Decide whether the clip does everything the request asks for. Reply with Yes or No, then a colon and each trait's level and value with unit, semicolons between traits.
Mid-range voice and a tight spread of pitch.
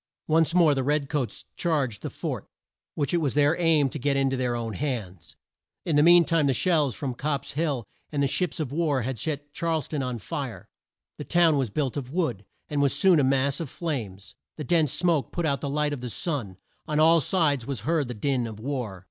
No: medium, 145 Hz; average, 3.8 semitones